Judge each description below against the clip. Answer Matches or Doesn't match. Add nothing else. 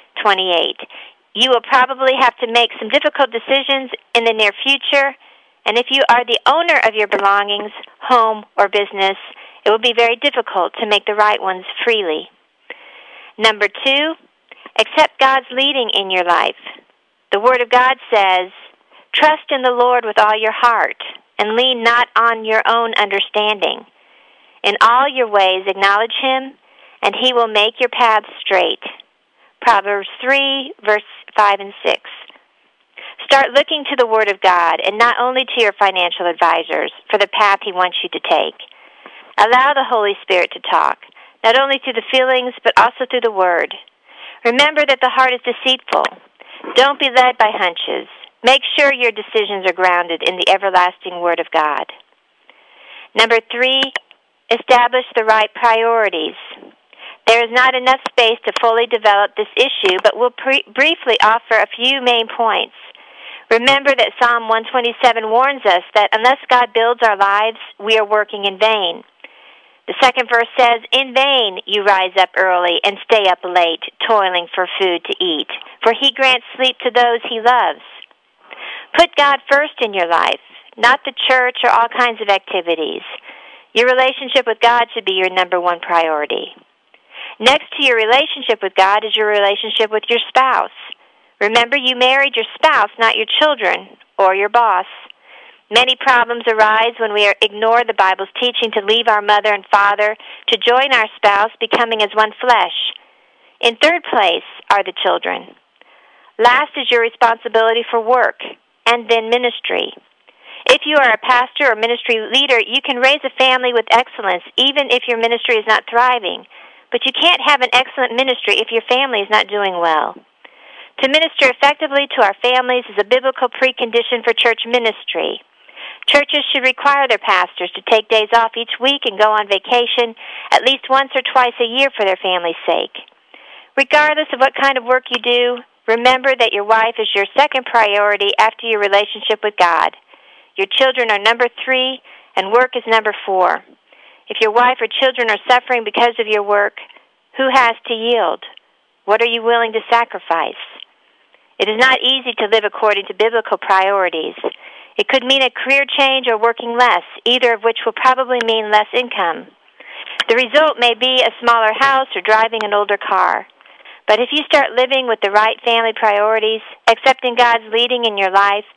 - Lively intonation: Doesn't match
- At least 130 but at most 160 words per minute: Doesn't match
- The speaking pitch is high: Matches